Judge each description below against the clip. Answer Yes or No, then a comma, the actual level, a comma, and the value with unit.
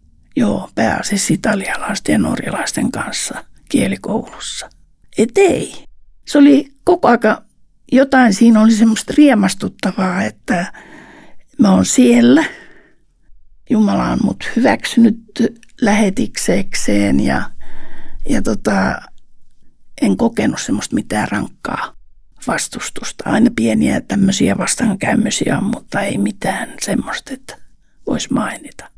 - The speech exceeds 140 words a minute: No, slow, 95 wpm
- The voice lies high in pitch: Yes, high, 225 Hz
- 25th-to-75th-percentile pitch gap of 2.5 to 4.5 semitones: No, average, 5.2 semitones